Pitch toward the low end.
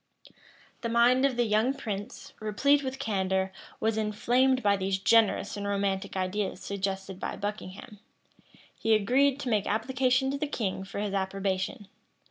No: high, 210 Hz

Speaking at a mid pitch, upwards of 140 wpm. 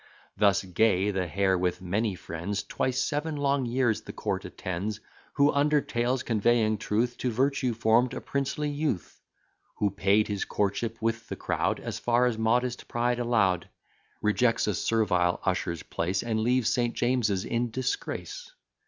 No: low, 115 Hz; average, 155 wpm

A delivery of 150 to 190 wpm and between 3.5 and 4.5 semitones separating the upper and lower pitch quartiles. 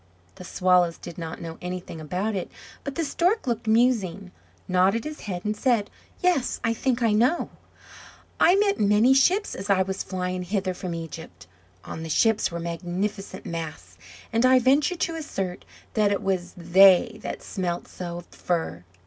No: average, 170 wpm; average, 5.2 semitones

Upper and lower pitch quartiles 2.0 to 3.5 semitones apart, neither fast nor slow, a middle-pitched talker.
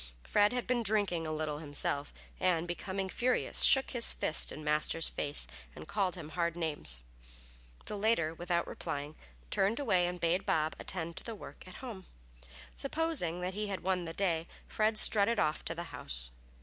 No: average, 4.5 semitones; average, 175 wpm; medium, 175 Hz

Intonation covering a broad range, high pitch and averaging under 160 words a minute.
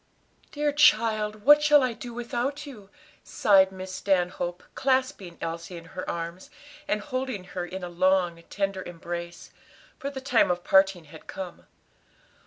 Yes: wide, 6.2 semitones; high, 195 Hz; average, 150 wpm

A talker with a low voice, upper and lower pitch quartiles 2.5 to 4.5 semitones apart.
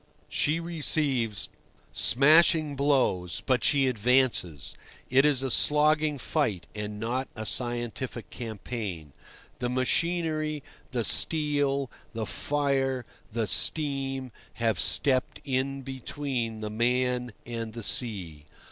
Yes: low, 130 Hz; average, 4.0 semitones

